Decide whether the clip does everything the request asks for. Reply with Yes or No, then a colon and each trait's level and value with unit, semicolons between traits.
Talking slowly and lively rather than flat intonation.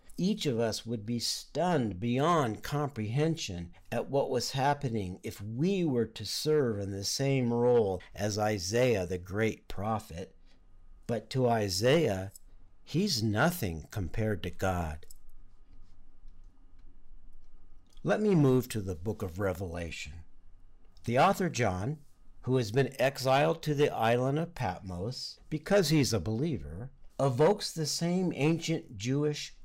Yes: slow, 130 wpm; wide, 7.2 semitones